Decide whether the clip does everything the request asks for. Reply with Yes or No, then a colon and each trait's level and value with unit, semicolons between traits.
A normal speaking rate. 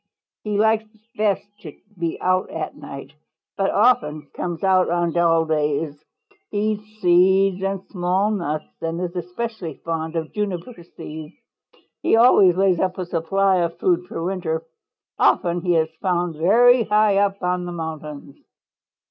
Yes: average, 150 wpm